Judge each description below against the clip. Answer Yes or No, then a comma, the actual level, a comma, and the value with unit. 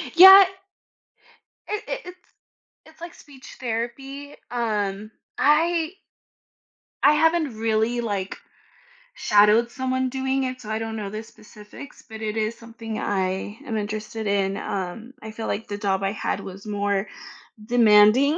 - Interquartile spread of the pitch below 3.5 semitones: No, average, 4.1 semitones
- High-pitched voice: Yes, high, 225 Hz